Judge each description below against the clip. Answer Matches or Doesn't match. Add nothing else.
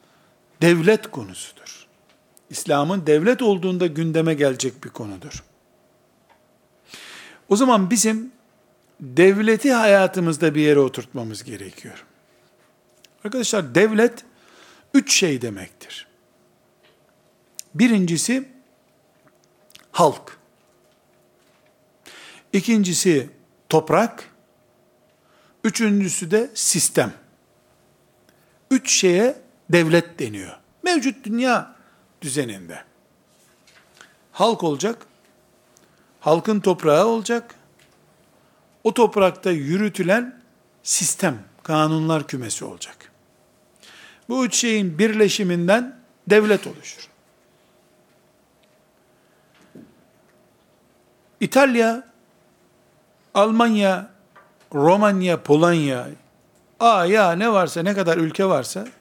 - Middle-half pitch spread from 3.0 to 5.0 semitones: Doesn't match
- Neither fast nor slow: Doesn't match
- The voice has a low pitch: Doesn't match